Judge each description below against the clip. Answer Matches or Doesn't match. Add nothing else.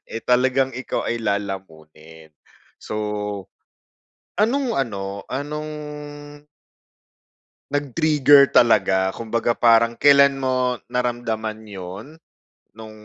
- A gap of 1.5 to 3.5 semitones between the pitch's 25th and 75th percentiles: Doesn't match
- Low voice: Matches